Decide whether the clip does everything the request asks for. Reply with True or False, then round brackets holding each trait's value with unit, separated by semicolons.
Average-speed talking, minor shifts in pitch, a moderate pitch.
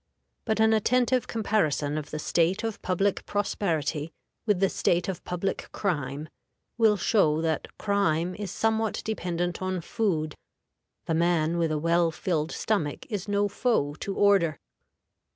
False (145 wpm; 4.3 semitones; 180 Hz)